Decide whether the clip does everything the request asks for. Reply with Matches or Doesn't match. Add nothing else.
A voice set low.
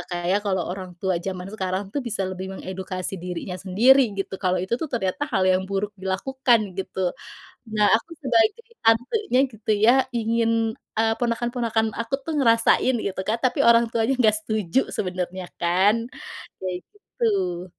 Doesn't match